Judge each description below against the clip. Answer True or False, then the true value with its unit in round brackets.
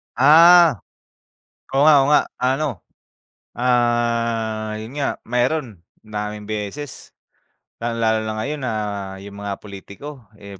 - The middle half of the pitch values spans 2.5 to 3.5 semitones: False (4.2 semitones)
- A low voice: True (115 Hz)